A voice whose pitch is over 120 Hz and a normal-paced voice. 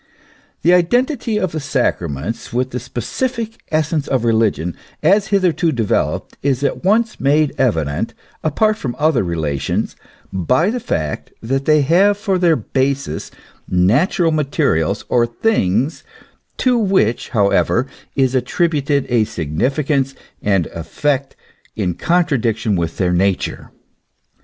No: low, 135 Hz; slow, 125 wpm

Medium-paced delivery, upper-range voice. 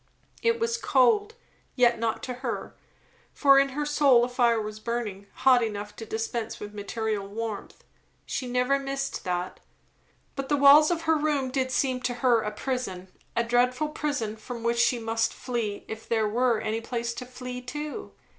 Yes: average, 175 wpm; high, 245 Hz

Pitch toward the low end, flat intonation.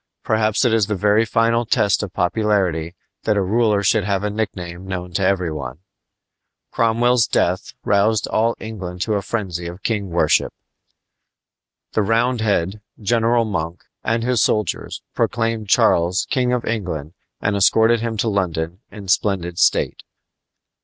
No: low, 105 Hz; average, 3.8 semitones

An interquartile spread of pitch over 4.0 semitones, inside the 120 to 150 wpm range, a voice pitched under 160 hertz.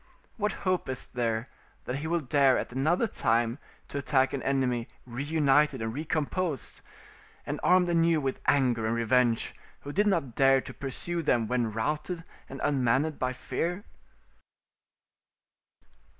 Yes: average, 4.5 semitones; average, 140 wpm; low, 135 Hz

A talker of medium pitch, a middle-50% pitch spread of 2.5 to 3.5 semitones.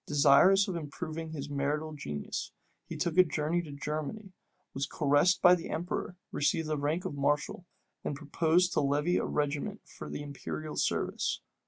Yes: medium, 155 Hz; average, 3.2 semitones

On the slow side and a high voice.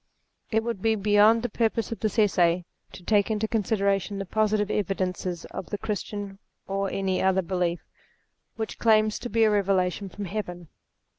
No: average, 165 wpm; high, 205 Hz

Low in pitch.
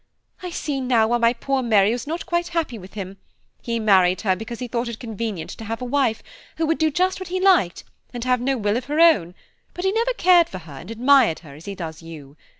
No: high, 235 Hz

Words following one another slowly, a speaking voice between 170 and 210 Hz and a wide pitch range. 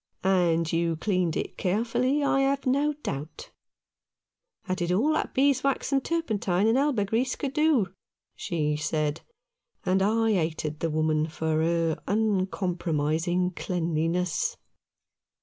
Yes: slow, 130 wpm; medium, 185 Hz; wide, 6.7 semitones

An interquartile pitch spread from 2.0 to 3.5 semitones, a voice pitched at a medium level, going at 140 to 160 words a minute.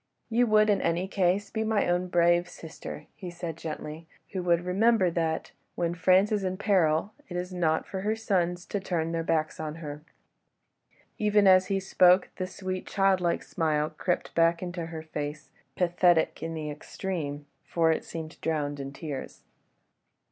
No: average, 2.8 semitones; medium, 175 Hz; average, 170 wpm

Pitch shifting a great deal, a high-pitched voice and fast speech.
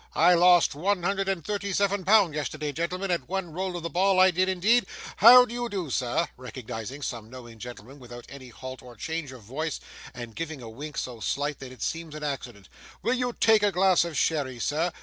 No: wide, 6.6 semitones; medium, 160 Hz; fast, 215 wpm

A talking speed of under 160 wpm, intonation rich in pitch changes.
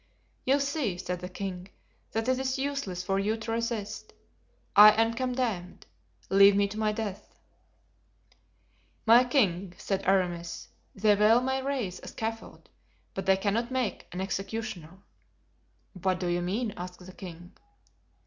No: average, 145 wpm; average, 4.0 semitones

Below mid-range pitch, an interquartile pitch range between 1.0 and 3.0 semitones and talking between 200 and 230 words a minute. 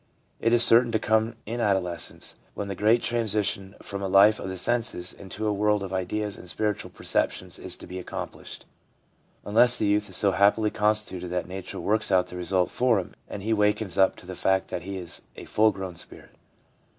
Yes: low, 100 Hz; narrow, 2.5 semitones; fast, 205 wpm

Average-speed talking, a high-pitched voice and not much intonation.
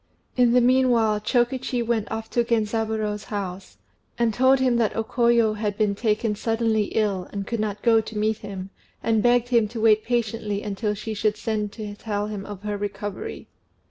Yes: average, 185 wpm; high, 220 Hz; narrow, 2.1 semitones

